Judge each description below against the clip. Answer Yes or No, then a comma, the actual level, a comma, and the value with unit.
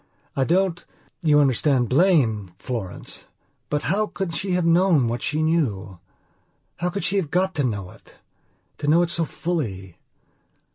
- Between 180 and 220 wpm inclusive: No, average, 155 wpm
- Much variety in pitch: Yes, wide, 6.5 semitones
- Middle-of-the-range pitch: Yes, medium, 155 Hz